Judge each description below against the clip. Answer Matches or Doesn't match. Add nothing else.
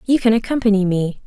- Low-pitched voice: Doesn't match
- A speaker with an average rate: Matches